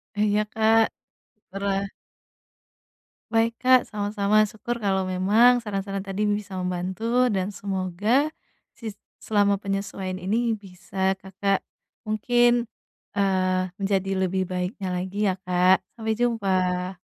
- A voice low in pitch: No, high, 200 Hz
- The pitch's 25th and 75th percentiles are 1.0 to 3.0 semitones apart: Yes, narrow, 2.6 semitones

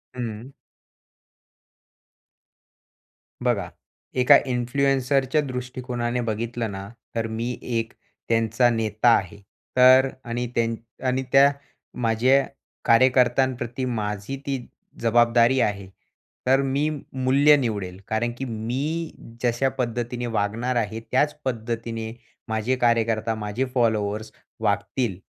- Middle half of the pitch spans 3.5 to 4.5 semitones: No, narrow, 2.6 semitones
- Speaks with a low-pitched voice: Yes, low, 120 Hz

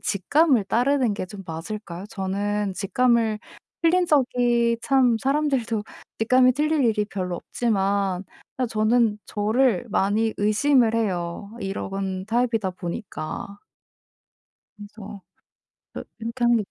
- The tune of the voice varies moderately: Yes, average, 3.8 semitones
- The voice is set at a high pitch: Yes, high, 220 Hz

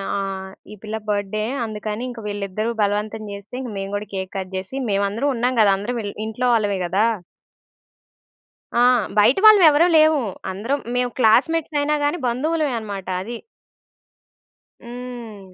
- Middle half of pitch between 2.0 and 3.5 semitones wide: No, average, 3.9 semitones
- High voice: Yes, high, 220 Hz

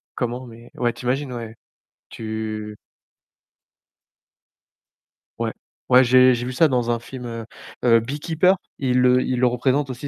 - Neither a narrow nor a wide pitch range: No, narrow, 1.6 semitones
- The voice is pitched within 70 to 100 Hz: No, low, 125 Hz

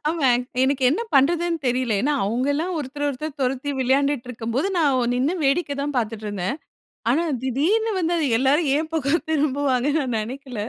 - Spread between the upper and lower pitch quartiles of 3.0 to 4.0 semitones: Yes, average, 3.4 semitones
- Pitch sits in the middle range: No, very high, 275 Hz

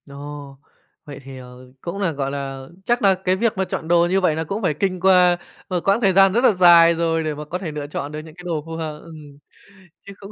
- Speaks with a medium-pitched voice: Yes, medium, 165 Hz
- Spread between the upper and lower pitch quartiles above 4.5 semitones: No, average, 4.2 semitones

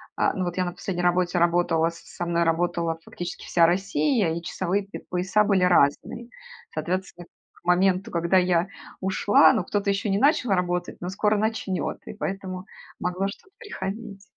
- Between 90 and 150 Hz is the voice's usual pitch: No, medium, 185 Hz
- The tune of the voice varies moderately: No, narrow, 2.2 semitones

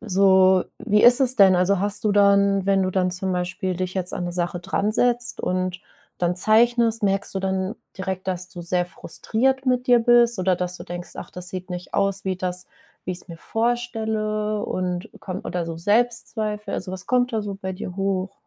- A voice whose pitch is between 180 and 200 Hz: Yes, high, 190 Hz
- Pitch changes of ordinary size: Yes, average, 3.0 semitones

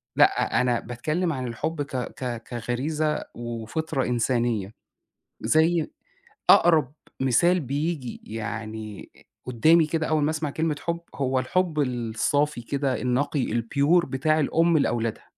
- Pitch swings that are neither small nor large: Yes, average, 4.7 semitones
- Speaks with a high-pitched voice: No, low, 135 Hz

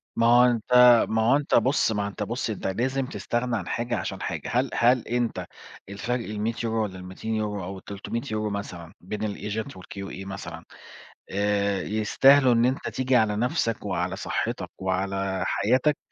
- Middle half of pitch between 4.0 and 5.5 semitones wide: No, average, 3.6 semitones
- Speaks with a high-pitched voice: No, low, 110 Hz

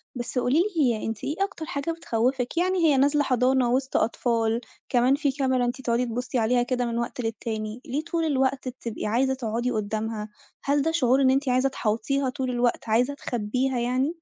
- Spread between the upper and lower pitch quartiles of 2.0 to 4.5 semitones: Yes, narrow, 2.6 semitones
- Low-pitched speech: No, very high, 250 Hz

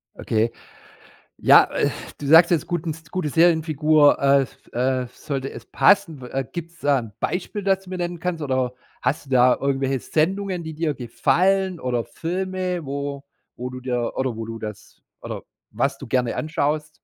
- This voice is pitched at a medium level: Yes, medium, 145 Hz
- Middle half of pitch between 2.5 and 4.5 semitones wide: No, average, 4.9 semitones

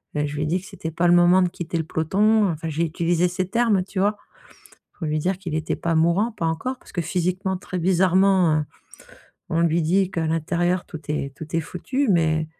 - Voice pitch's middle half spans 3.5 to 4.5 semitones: No, average, 2.7 semitones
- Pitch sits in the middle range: Yes, medium, 175 Hz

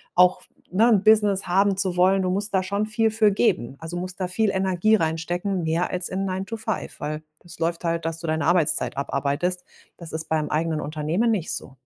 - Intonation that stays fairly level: No, average, 3.4 semitones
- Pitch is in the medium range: Yes, medium, 180 Hz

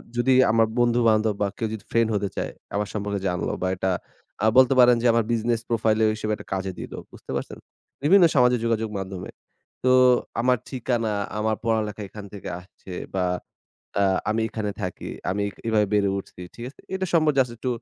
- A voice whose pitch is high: No, low, 110 Hz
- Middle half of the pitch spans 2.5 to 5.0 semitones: Yes, average, 2.8 semitones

